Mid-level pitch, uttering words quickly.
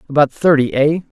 No: medium, 145 Hz; average, 150 wpm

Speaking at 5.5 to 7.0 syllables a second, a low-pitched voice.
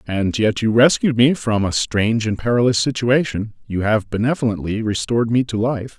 No: 5.2 syllables/s; low, 115 Hz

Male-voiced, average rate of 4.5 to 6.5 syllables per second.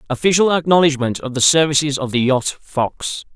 Yes: male; 5.2 syllables/s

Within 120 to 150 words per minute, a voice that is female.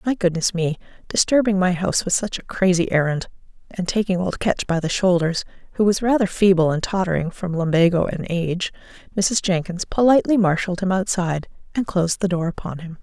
No: average, 185 wpm; female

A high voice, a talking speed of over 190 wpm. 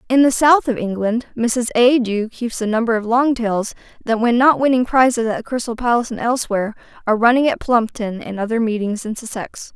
Yes: high, 230 Hz; fast, 205 wpm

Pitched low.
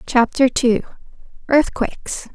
No: very high, 250 Hz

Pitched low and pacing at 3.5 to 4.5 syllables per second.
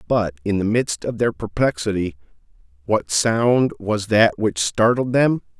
Yes: low, 105 Hz; 4.1 syllables/s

